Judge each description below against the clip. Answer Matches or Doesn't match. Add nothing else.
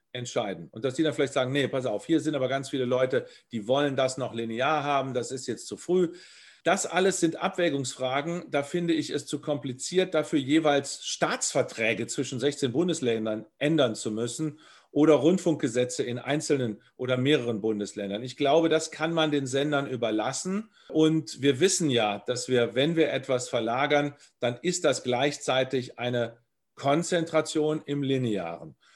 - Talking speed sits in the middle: Matches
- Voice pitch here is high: Doesn't match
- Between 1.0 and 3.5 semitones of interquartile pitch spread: Doesn't match